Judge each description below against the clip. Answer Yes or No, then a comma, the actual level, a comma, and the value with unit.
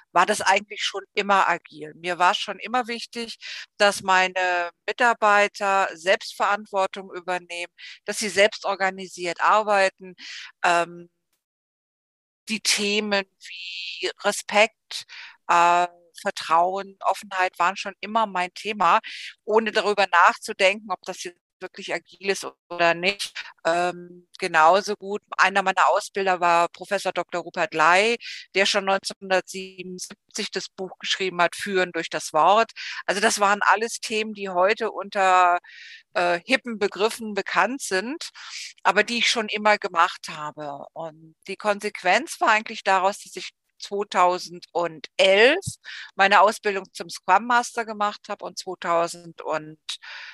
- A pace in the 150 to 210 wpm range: No, slow, 125 wpm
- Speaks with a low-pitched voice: No, high, 190 Hz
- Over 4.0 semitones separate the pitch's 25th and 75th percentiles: No, average, 2.8 semitones